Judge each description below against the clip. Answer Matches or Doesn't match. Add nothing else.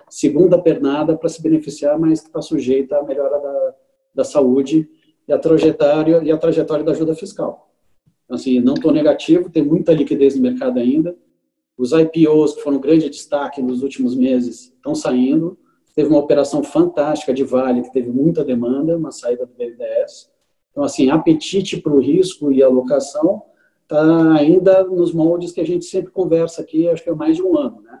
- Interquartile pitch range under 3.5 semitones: Doesn't match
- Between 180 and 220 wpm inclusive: Matches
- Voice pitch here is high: Doesn't match